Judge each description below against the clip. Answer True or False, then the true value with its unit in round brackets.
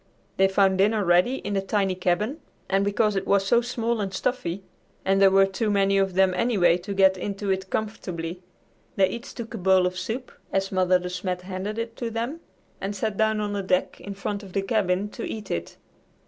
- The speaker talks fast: True (215 wpm)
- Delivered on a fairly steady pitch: True (2.3 semitones)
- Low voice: False (195 Hz)